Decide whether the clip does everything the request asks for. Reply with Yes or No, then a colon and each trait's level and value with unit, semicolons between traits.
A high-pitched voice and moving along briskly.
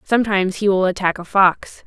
No: high, 195 Hz; average, 195 wpm